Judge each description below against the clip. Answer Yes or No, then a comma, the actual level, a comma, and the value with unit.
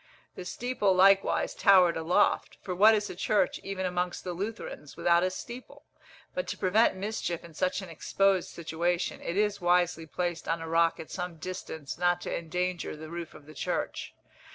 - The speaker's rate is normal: Yes, average, 180 wpm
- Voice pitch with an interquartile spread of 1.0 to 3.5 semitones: Yes, narrow, 2.5 semitones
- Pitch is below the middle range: No, medium, 180 Hz